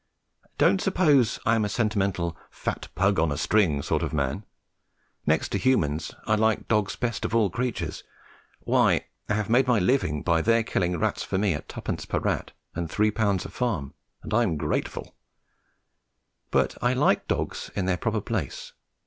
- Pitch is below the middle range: Yes, low, 100 Hz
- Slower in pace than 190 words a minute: Yes, average, 180 wpm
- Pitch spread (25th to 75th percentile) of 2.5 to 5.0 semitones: No, wide, 5.6 semitones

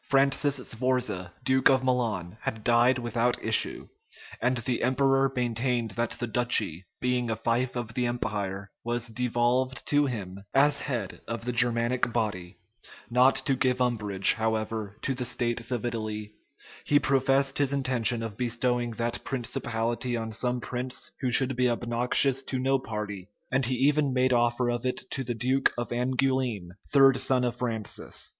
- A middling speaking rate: Yes, average, 160 wpm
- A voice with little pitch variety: Yes, narrow, 2.2 semitones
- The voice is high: No, low, 120 Hz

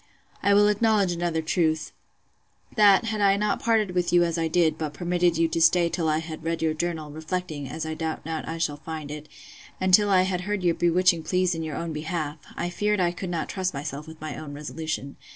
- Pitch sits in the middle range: Yes, medium, 170 Hz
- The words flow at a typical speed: No, fast, 225 wpm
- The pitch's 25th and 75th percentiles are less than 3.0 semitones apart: Yes, narrow, 2.6 semitones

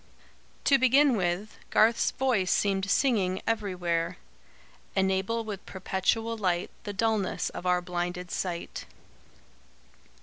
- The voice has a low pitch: No, high, 195 Hz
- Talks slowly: Yes, slow, 105 wpm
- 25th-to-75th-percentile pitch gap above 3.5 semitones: Yes, average, 3.9 semitones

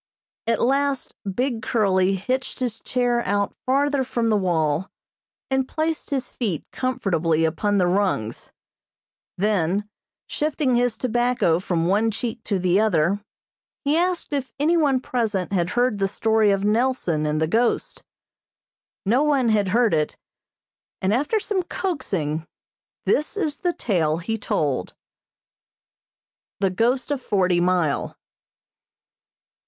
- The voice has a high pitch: Yes, high, 220 Hz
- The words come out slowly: Yes, slow, 130 wpm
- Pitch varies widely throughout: Yes, wide, 5.9 semitones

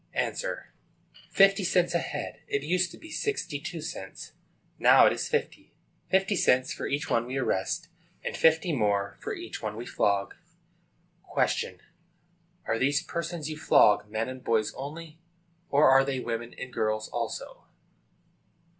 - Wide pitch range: Yes, wide, 6.7 semitones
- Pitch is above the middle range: No, medium, 140 Hz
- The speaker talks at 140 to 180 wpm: Yes, average, 155 wpm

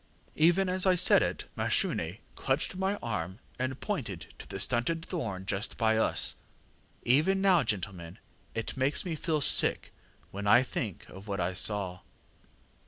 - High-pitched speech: No, low, 120 Hz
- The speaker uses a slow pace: No, average, 160 wpm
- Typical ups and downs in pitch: No, wide, 8.9 semitones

